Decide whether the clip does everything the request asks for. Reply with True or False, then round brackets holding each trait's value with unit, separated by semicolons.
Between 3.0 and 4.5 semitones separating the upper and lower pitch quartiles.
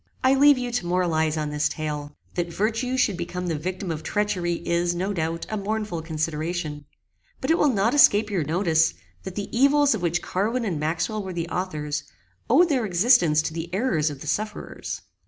False (5.1 semitones)